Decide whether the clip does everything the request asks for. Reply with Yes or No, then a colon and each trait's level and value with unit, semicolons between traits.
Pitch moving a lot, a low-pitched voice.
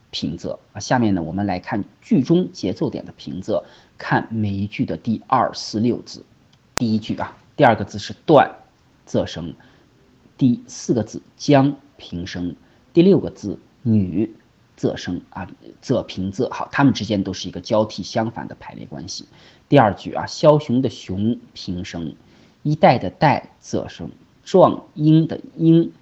Yes: wide, 6.0 semitones; low, 110 Hz